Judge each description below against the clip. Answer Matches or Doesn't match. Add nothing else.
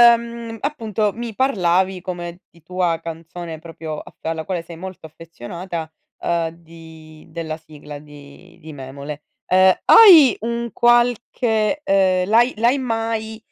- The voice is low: Doesn't match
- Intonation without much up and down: Doesn't match